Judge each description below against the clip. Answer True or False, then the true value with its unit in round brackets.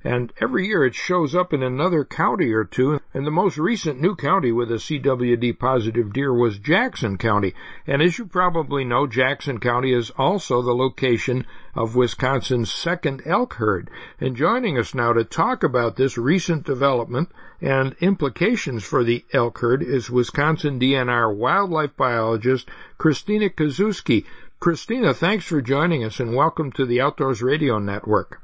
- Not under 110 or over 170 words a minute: True (160 wpm)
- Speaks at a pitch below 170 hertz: True (135 Hz)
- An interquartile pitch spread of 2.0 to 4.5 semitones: False (5.0 semitones)